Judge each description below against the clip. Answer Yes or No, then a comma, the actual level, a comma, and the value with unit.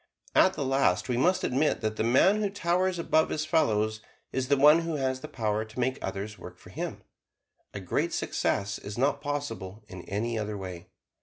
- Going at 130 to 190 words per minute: No, average, 200 wpm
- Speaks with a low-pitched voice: Yes, low, 125 Hz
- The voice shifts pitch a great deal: Yes, wide, 6.1 semitones